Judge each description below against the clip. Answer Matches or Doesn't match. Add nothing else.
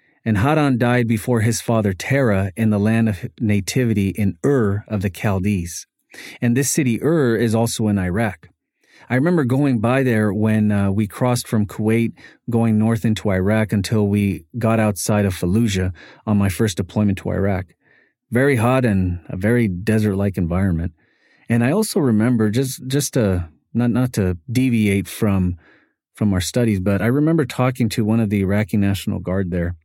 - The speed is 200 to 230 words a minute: Doesn't match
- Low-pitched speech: Matches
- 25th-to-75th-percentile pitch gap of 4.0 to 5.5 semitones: Doesn't match